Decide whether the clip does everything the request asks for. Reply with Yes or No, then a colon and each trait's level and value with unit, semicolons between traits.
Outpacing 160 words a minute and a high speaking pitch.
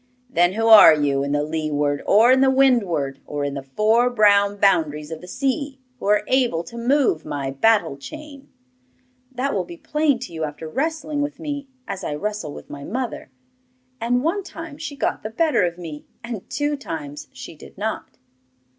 Yes: average, 190 wpm; high, 210 Hz